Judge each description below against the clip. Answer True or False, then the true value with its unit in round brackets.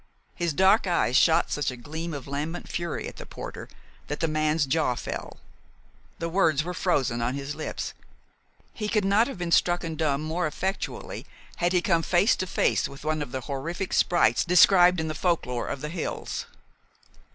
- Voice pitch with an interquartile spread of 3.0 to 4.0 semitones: True (3.4 semitones)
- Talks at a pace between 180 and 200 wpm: True (185 wpm)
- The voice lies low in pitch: False (165 Hz)